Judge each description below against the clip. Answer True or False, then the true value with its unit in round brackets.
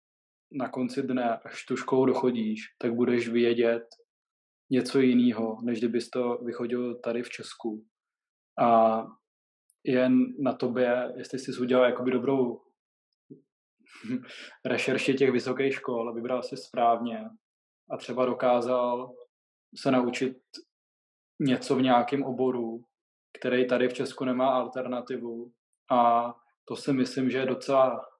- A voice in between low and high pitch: False (125 Hz)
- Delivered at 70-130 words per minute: True (125 wpm)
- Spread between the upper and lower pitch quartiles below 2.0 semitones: True (1.5 semitones)